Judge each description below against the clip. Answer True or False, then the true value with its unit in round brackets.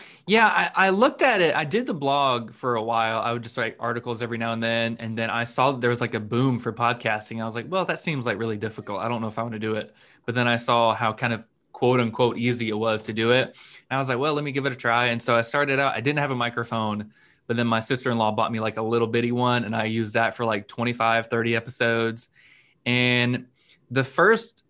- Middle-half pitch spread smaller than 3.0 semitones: True (2.5 semitones)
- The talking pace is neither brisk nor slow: False (275 wpm)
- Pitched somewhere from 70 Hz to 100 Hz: False (120 Hz)